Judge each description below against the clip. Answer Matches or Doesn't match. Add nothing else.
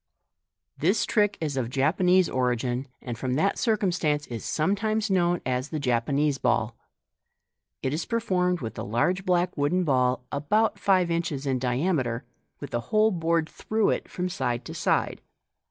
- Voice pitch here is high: Doesn't match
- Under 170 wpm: Matches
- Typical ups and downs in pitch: Doesn't match